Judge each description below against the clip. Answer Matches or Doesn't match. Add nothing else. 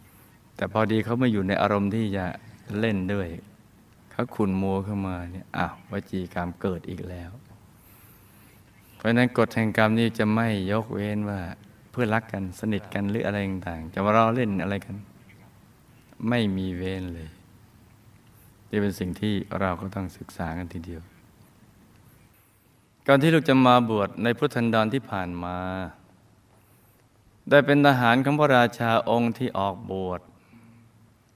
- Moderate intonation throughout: Matches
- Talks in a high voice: Doesn't match